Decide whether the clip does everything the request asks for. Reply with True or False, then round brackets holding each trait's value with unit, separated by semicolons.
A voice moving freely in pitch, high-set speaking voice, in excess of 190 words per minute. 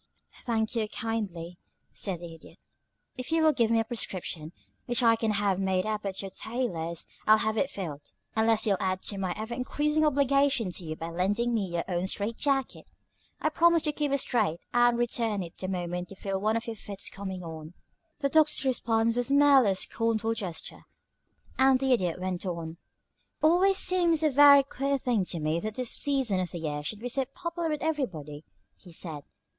True (6.4 semitones; 220 Hz; 200 wpm)